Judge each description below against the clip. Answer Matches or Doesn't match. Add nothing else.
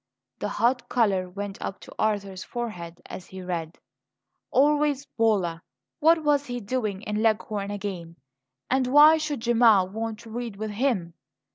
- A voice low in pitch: Doesn't match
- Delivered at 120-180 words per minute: Matches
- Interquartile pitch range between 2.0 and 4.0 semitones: Doesn't match